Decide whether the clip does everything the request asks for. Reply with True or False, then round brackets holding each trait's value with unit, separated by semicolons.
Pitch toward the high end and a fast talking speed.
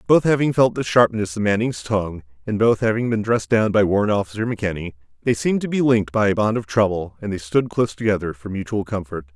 False (105 Hz; 230 wpm)